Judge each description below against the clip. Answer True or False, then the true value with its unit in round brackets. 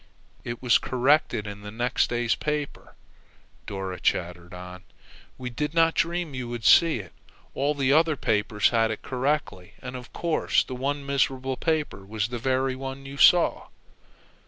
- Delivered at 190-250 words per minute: False (155 wpm)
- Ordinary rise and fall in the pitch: True (4.6 semitones)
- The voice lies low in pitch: True (130 Hz)